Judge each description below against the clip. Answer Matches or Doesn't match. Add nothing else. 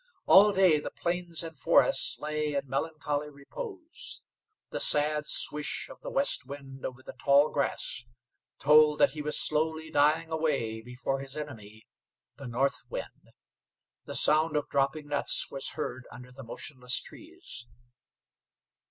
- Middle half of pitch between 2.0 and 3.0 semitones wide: Matches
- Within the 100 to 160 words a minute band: Matches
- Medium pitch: Matches